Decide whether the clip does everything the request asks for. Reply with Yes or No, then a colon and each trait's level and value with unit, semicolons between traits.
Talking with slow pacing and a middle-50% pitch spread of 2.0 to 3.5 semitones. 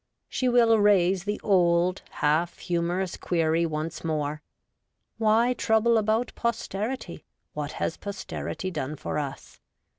No: slow, 125 wpm; average, 5.1 semitones